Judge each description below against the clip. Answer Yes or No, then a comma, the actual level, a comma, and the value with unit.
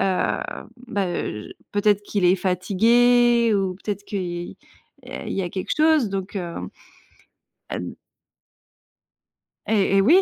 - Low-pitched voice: No, high, 195 Hz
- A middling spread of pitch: Yes, average, 3.4 semitones